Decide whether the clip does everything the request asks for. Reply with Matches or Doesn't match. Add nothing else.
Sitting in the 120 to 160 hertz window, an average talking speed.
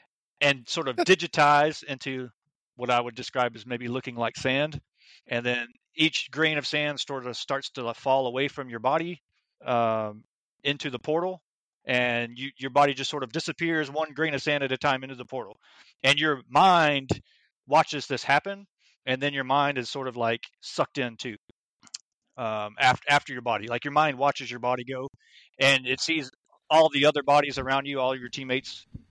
Matches